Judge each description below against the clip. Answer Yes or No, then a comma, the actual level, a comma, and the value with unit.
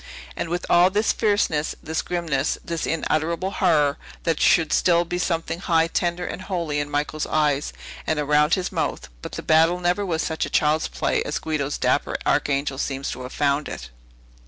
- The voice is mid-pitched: Yes, medium, 160 Hz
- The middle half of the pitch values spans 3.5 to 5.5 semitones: No, average, 3.0 semitones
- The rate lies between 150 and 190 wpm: Yes, average, 180 wpm